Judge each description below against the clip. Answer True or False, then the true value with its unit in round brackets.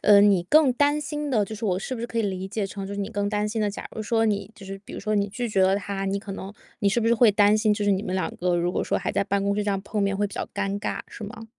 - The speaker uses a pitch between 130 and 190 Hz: False (205 Hz)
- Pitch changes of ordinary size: False (2.0 semitones)